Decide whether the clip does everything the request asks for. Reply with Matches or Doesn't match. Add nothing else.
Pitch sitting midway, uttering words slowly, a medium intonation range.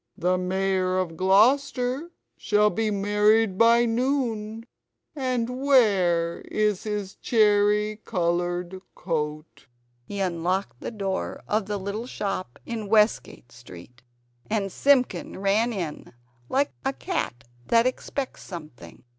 Doesn't match